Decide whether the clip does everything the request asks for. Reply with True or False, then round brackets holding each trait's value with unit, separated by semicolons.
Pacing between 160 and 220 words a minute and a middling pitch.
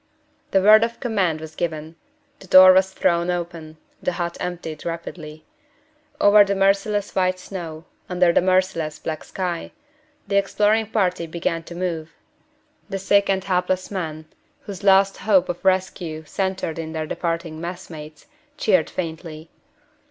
False (145 wpm; 180 Hz)